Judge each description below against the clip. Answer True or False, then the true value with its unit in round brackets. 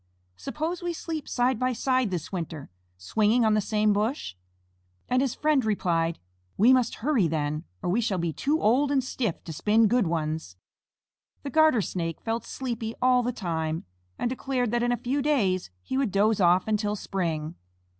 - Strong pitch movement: True (6.3 semitones)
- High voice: True (220 Hz)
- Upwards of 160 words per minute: True (180 wpm)